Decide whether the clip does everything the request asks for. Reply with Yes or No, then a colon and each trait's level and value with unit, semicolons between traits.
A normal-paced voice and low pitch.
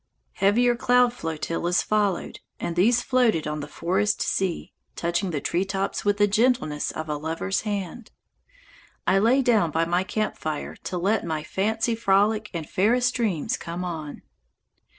No: average, 150 wpm; high, 195 Hz